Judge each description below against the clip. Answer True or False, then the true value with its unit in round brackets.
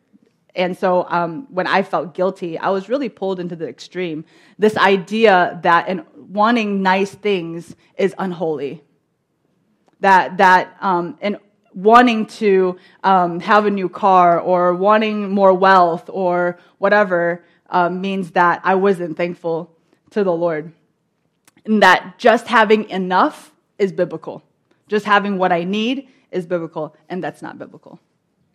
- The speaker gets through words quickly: False (135 wpm)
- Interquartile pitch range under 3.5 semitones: True (2.8 semitones)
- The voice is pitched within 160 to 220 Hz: True (185 Hz)